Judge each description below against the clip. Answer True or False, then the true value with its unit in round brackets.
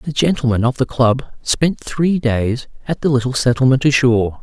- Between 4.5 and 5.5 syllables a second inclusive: True (5.0 syllables/s)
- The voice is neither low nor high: False (130 Hz)